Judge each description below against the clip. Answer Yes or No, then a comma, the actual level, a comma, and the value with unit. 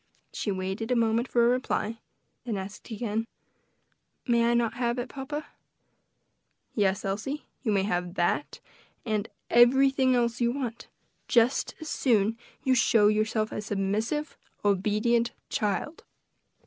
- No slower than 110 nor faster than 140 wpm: Yes, slow, 135 wpm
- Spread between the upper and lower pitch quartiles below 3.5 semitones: Yes, average, 2.9 semitones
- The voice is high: Yes, high, 230 Hz